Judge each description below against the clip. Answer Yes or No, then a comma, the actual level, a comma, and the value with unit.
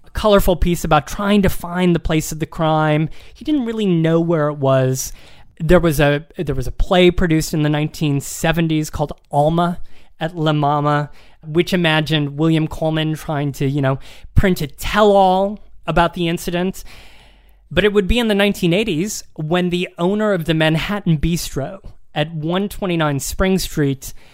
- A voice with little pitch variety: No, average, 3.3 semitones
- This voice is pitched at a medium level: Yes, medium, 160 Hz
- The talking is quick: No, average, 170 wpm